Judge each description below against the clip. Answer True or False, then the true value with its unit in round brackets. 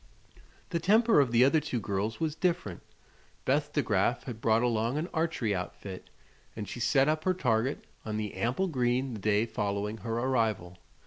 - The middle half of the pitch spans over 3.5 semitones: True (5.5 semitones)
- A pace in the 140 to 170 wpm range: False (180 wpm)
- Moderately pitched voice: False (120 Hz)